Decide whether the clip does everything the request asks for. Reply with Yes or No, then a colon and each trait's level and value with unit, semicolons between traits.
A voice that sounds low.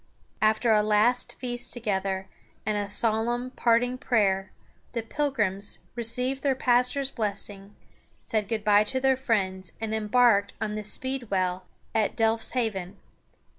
No: high, 220 Hz